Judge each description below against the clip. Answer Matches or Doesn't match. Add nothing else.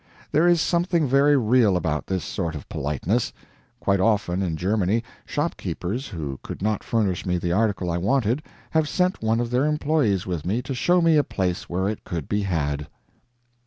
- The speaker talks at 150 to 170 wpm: Doesn't match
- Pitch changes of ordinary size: Doesn't match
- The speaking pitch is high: Doesn't match